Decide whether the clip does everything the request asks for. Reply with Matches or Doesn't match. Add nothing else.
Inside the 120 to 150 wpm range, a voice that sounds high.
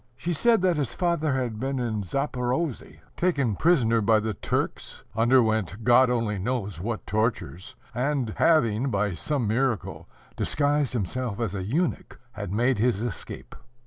Doesn't match